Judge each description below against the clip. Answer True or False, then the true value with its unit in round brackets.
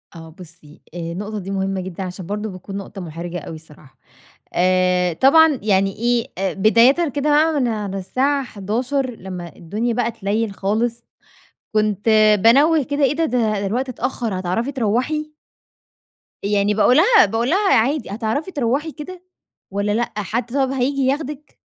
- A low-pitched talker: False (225 Hz)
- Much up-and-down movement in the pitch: True (5.8 semitones)